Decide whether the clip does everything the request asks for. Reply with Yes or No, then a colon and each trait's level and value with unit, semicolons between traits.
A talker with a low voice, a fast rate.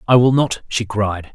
Yes: low, 110 Hz; fast, 225 wpm